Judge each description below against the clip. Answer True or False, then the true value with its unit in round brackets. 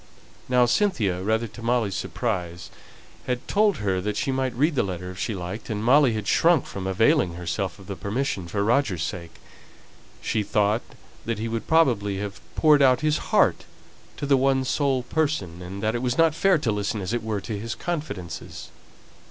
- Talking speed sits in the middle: True (190 wpm)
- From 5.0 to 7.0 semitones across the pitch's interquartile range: True (5.5 semitones)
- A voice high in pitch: False (110 Hz)